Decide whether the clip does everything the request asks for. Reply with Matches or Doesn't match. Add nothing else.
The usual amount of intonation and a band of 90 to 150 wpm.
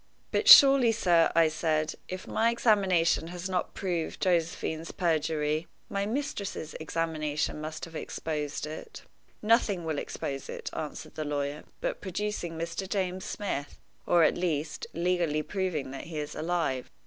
Matches